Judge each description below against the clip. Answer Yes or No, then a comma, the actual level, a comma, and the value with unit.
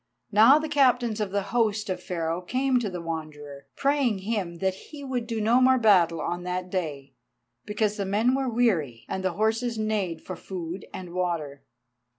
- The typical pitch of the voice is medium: No, high, 200 Hz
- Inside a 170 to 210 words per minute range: Yes, average, 180 wpm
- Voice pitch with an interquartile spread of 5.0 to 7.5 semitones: Yes, average, 5.3 semitones